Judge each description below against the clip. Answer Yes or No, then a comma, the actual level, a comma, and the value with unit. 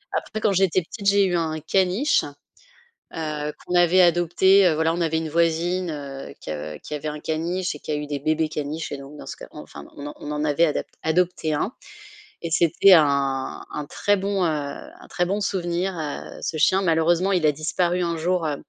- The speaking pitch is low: No, medium, 165 Hz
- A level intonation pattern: No, average, 3.2 semitones